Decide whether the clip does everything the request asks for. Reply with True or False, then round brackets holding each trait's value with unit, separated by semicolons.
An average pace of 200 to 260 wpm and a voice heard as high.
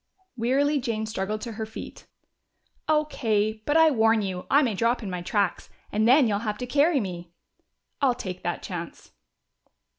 False (170 wpm; 220 Hz)